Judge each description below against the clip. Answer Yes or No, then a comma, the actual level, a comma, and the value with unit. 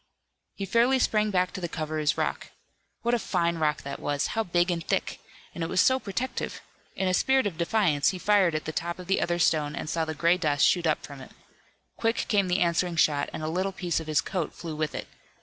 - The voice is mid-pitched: Yes, medium, 170 Hz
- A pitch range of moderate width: Yes, average, 3.7 semitones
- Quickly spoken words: Yes, fast, 245 wpm